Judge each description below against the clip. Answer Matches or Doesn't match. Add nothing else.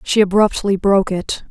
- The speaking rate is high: Doesn't match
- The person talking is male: Doesn't match